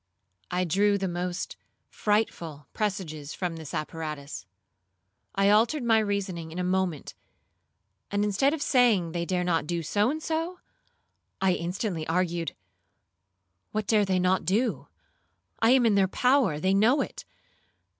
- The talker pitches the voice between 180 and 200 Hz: Yes, high, 190 Hz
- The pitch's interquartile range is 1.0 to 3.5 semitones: No, average, 4.1 semitones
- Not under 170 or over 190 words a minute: No, average, 140 wpm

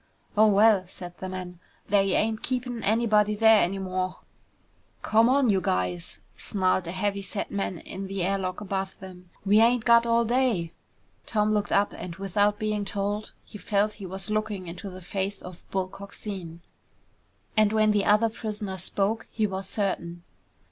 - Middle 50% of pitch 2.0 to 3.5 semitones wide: Yes, narrow, 2.5 semitones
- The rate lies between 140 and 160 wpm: No, average, 170 wpm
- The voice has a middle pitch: No, high, 200 Hz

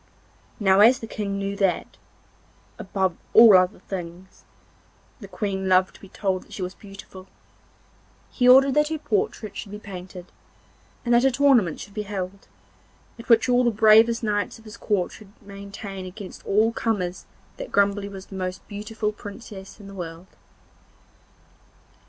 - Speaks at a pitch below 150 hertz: No, high, 200 Hz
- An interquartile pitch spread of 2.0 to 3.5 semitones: Yes, average, 2.8 semitones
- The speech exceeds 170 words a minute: No, average, 160 wpm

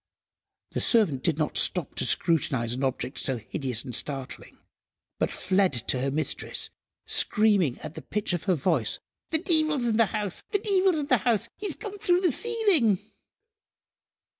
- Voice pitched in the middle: No, high, 195 Hz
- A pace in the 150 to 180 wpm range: Yes, average, 165 wpm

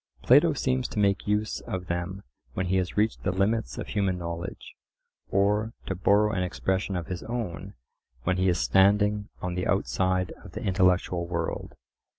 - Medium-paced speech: Yes, average, 170 wpm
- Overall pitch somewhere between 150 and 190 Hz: No, very low, 95 Hz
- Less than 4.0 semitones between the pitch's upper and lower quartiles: Yes, narrow, 2.4 semitones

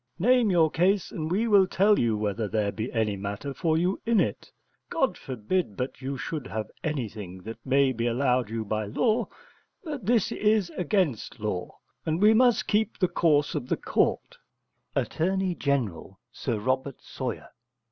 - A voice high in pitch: No, medium, 140 Hz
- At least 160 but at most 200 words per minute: Yes, average, 165 wpm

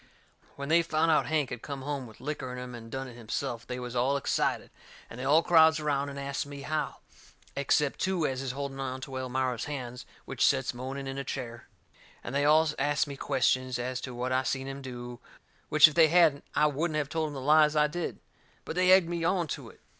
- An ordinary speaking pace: No, fast, 230 wpm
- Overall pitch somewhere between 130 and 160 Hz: Yes, medium, 140 Hz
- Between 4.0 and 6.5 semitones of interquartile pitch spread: No, average, 3.0 semitones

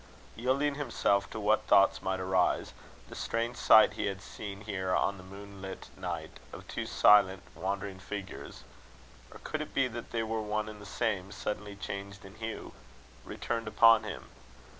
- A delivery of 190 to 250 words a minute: No, average, 165 wpm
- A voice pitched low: Yes, low, 105 Hz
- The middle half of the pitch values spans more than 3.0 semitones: No, narrow, 2.4 semitones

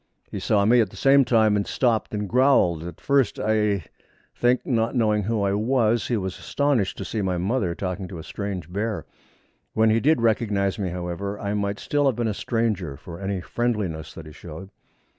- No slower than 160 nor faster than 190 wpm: No, average, 200 wpm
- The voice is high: No, low, 105 Hz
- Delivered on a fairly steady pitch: No, average, 3.5 semitones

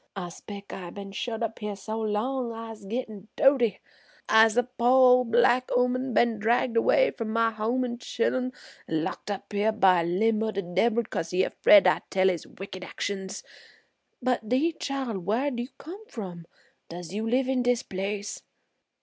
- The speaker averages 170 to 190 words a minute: Yes, average, 175 wpm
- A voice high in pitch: Yes, high, 225 Hz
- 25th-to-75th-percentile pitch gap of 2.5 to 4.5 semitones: Yes, average, 3.8 semitones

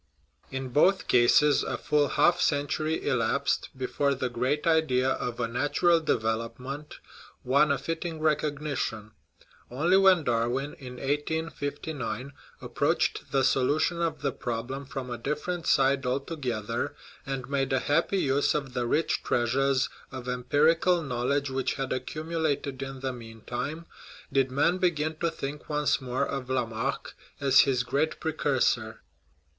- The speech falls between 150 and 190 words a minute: No, average, 140 wpm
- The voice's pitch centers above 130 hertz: Yes, medium, 140 Hz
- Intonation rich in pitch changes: No, average, 3.2 semitones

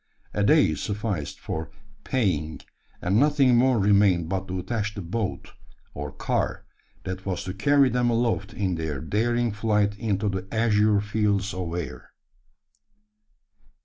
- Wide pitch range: No, average, 3.7 semitones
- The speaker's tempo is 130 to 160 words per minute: Yes, average, 140 wpm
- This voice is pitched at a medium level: No, low, 100 Hz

